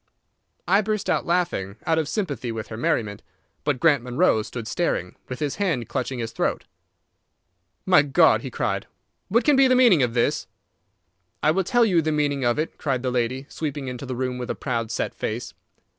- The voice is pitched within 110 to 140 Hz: Yes, low, 135 Hz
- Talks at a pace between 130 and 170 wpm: No, average, 195 wpm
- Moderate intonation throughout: No, wide, 5.7 semitones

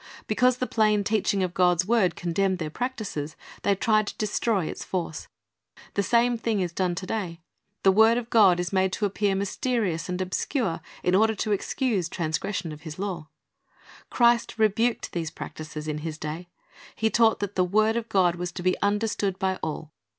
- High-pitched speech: Yes, high, 195 Hz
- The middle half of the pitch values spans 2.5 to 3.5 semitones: No, average, 3.9 semitones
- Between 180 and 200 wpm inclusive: Yes, average, 185 wpm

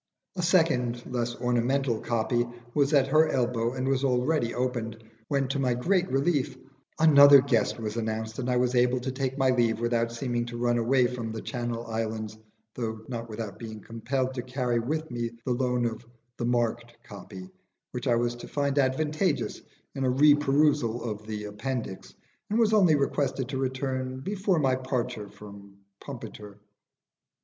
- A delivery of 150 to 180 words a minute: Yes, average, 170 wpm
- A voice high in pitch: No, low, 125 Hz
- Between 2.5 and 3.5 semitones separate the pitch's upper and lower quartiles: Yes, average, 2.8 semitones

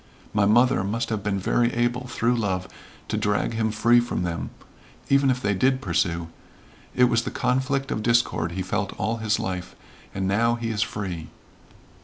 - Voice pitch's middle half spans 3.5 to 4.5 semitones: Yes, average, 3.9 semitones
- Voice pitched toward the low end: Yes, low, 110 Hz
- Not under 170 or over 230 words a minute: Yes, average, 180 wpm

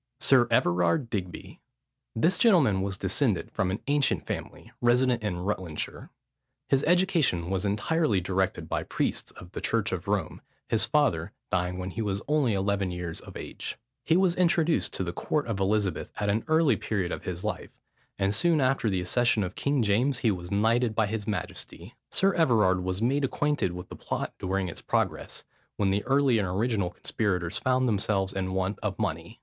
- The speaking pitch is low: Yes, low, 105 Hz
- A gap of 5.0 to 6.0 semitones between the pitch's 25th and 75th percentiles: Yes, wide, 5.6 semitones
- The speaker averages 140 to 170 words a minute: No, average, 180 wpm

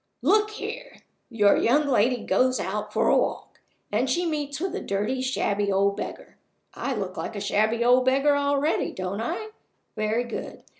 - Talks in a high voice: Yes, very high, 255 Hz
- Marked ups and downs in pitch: Yes, wide, 5.7 semitones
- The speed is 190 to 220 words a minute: No, average, 170 wpm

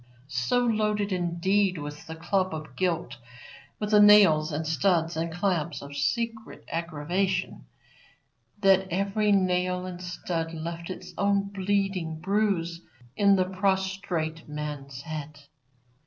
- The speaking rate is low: Yes, slow, 125 wpm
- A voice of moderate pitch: Yes, medium, 180 Hz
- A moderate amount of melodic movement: Yes, average, 3.5 semitones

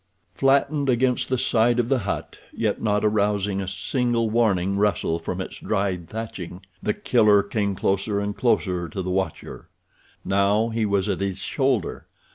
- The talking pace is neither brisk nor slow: Yes, average, 160 wpm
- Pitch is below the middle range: Yes, low, 105 Hz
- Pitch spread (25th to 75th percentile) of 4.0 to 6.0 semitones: No, average, 3.2 semitones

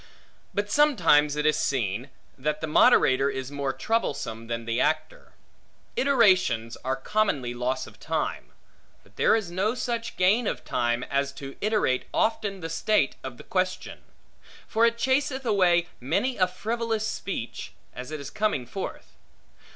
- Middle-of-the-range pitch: Yes, medium, 165 Hz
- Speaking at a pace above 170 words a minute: No, average, 150 wpm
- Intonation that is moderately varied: No, wide, 8.4 semitones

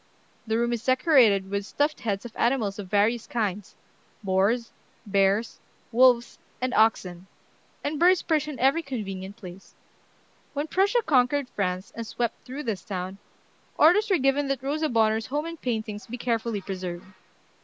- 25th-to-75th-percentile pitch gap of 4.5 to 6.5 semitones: Yes, wide, 5.4 semitones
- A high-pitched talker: Yes, high, 230 Hz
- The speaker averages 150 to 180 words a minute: Yes, average, 155 wpm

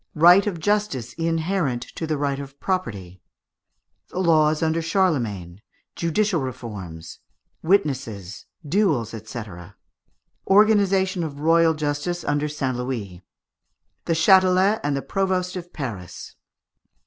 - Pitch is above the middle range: No, medium, 155 Hz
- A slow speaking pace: Yes, slow, 115 wpm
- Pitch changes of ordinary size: No, wide, 6.7 semitones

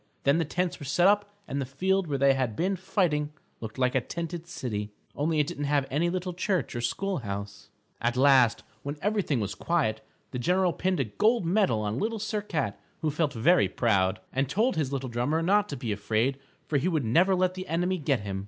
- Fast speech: Yes, fast, 220 wpm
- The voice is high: No, medium, 150 Hz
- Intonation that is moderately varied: No, wide, 6.6 semitones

